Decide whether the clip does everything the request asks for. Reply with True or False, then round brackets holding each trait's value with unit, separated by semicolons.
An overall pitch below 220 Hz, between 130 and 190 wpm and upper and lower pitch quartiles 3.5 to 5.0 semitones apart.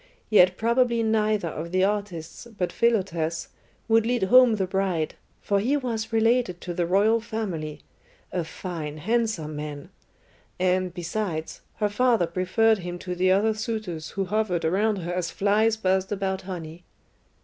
True (190 Hz; 150 wpm; 4.0 semitones)